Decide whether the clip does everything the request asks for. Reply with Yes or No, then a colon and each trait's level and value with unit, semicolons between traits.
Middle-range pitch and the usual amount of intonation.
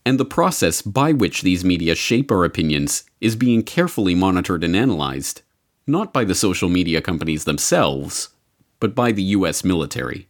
No: very low, 90 Hz; average, 5.0 semitones